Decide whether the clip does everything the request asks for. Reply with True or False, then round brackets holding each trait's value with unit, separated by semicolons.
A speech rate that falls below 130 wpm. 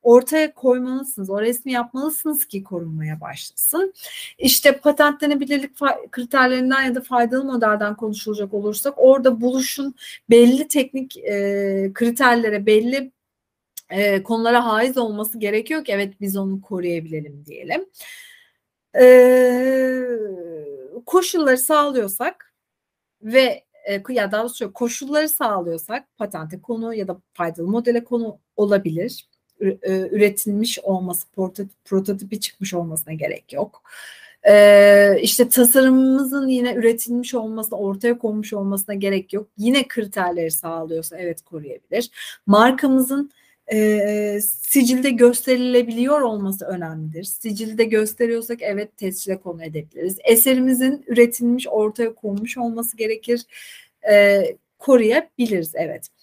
True (105 wpm)